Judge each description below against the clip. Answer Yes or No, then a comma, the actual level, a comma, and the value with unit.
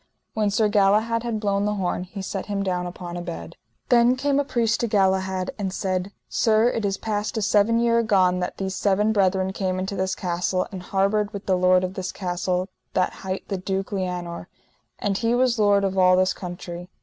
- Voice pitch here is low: No, high, 195 Hz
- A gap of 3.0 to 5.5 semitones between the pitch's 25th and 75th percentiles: No, narrow, 2.4 semitones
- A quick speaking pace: Yes, fast, 210 wpm